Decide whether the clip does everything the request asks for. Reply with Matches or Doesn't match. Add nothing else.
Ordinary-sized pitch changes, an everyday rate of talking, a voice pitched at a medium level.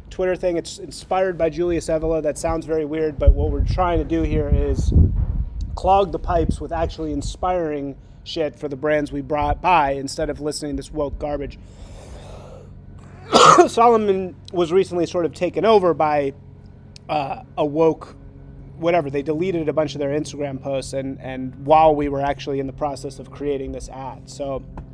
Matches